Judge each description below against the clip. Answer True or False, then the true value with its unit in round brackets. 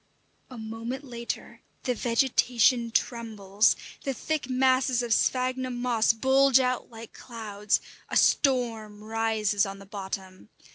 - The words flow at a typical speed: False (125 wpm)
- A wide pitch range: False (2.9 semitones)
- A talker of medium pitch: False (235 Hz)